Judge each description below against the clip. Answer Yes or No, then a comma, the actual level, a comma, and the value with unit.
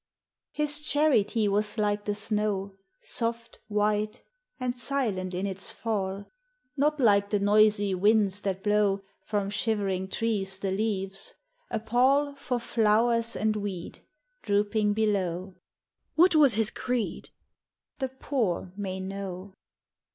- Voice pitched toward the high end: Yes, high, 210 Hz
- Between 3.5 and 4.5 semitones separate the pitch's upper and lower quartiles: No, average, 2.8 semitones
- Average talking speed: No, slow, 125 wpm